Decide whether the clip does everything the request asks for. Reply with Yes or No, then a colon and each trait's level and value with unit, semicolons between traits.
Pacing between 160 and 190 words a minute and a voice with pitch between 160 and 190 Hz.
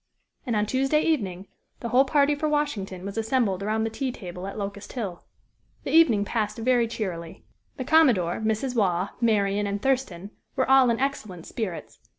No: average, 170 wpm; high, 220 Hz